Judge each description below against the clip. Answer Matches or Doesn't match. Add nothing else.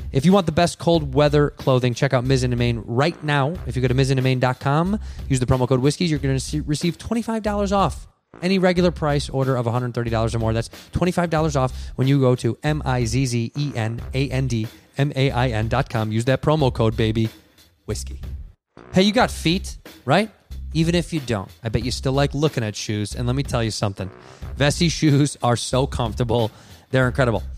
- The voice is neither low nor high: Doesn't match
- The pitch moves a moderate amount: Matches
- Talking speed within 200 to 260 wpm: Matches